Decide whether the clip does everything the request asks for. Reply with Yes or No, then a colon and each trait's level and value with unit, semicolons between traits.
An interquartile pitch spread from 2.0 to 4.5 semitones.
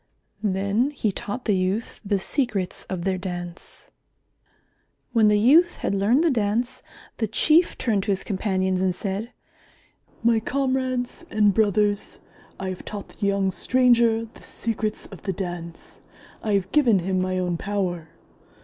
Yes: average, 3.6 semitones